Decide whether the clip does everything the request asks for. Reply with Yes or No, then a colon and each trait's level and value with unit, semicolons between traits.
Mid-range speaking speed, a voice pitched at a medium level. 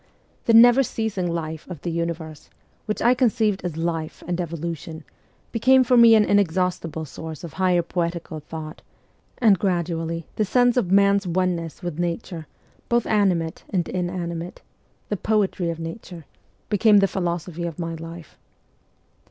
Yes: average, 145 wpm; medium, 175 Hz